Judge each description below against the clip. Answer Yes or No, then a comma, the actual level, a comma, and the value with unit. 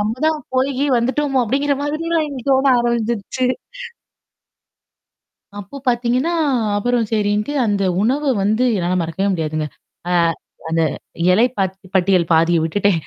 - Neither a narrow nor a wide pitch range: No, wide, 5.8 semitones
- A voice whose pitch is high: Yes, high, 225 Hz